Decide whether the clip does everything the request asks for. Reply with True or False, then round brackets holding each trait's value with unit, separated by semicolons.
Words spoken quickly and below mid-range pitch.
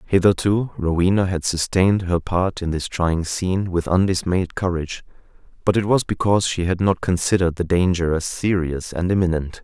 False (170 wpm; 90 Hz)